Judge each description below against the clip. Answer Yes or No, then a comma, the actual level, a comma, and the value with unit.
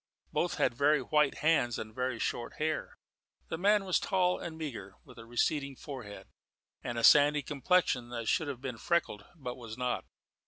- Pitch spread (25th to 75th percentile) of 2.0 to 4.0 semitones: No, average, 4.8 semitones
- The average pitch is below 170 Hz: Yes, medium, 140 Hz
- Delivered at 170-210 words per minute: Yes, average, 180 wpm